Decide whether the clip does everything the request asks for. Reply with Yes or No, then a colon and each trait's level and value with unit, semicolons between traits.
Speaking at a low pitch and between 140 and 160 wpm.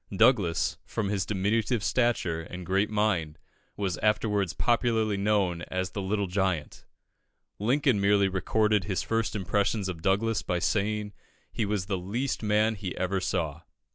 Yes: low, 100 Hz; average, 145 wpm